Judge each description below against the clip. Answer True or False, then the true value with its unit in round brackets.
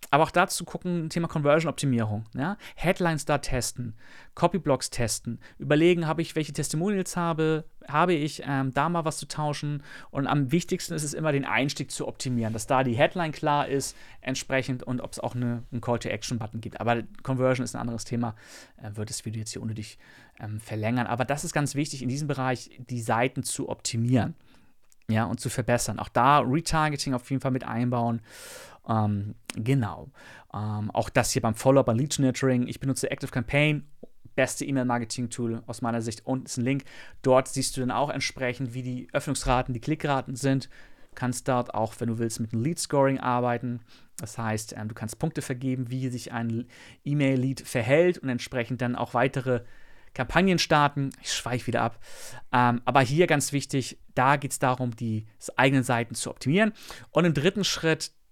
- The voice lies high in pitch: False (130 Hz)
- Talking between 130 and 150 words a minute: False (185 wpm)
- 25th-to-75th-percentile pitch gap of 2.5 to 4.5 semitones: True (3.5 semitones)